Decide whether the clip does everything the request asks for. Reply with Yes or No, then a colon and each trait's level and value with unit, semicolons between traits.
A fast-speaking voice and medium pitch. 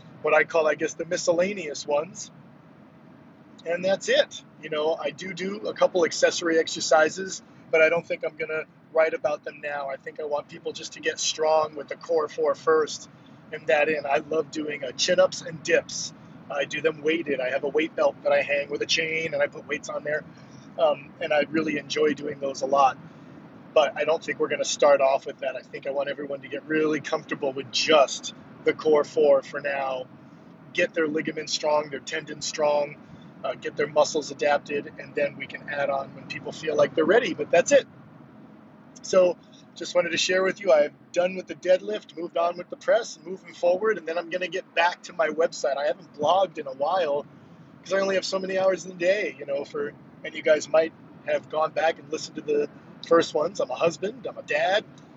Yes: fast, 220 wpm; medium, 160 Hz